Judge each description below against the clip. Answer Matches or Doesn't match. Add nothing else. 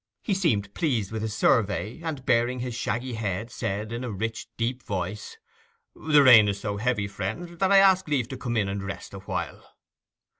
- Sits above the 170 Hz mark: Doesn't match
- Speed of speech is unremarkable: Matches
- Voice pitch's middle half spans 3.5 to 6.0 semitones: Matches